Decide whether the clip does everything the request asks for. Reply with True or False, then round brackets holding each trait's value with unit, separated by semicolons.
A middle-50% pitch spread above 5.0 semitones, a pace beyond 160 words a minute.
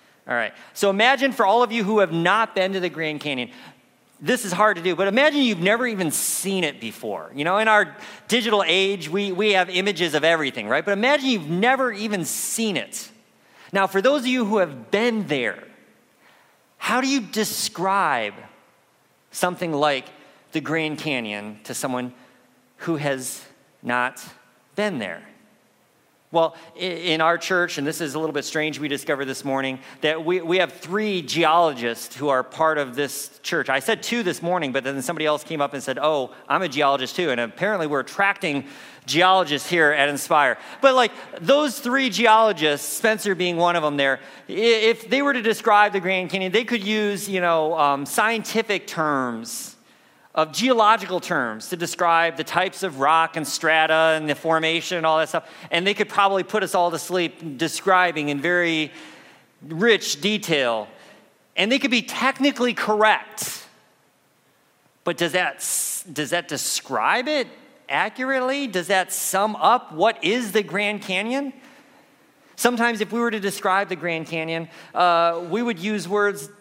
True (5.4 semitones; 175 wpm)